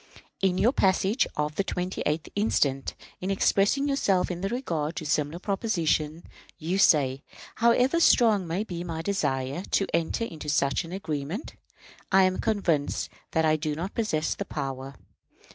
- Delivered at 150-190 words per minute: Yes, average, 155 wpm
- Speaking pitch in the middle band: Yes, medium, 175 Hz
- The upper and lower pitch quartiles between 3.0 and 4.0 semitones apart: No, average, 4.6 semitones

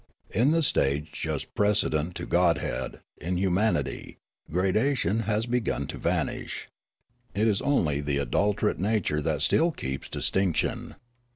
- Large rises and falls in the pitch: Yes, wide, 6.1 semitones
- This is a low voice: Yes, very low, 95 Hz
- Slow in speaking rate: Yes, slow, 125 wpm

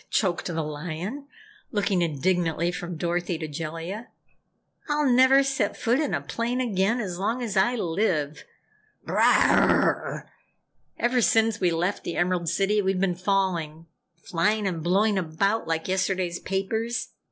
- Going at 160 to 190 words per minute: No, average, 140 wpm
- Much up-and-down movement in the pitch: No, average, 4.5 semitones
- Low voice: No, high, 190 Hz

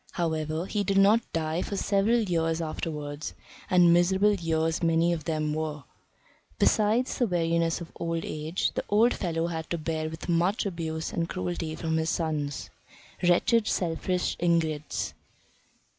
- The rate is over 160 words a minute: No, average, 145 wpm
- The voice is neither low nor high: Yes, medium, 165 Hz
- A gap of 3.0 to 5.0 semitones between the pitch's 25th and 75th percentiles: No, narrow, 2.4 semitones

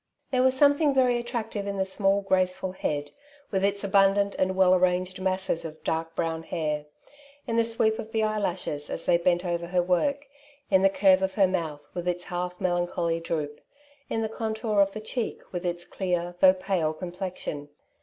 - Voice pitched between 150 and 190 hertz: Yes, medium, 185 Hz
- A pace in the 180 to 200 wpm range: Yes, average, 190 wpm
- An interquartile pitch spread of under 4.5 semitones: Yes, average, 2.8 semitones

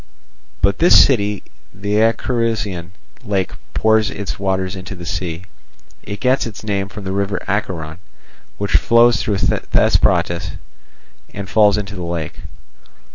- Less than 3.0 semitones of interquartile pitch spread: Yes, narrow, 2.5 semitones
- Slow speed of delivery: Yes, slow, 130 wpm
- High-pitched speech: No, low, 100 Hz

